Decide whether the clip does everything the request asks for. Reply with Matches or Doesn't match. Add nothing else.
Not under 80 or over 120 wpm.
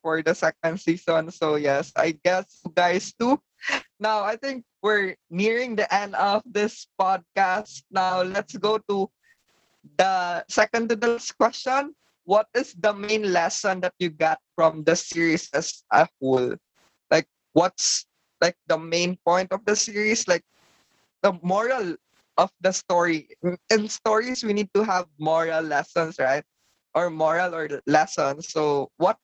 Doesn't match